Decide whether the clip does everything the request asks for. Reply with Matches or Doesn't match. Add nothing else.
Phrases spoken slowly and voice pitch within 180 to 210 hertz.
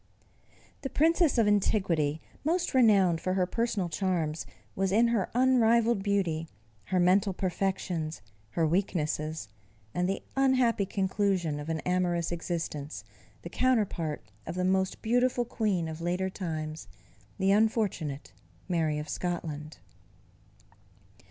Matches